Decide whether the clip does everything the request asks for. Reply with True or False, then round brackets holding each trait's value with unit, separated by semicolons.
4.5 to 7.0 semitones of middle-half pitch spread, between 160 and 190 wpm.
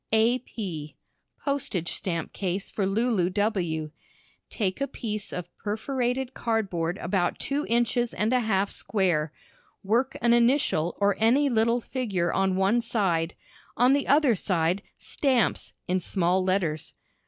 False (4.9 semitones; 140 wpm)